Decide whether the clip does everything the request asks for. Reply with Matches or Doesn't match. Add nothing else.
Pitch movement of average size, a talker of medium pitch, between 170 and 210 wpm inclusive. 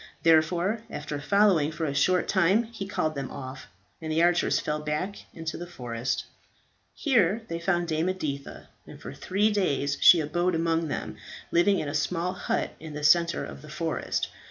Matches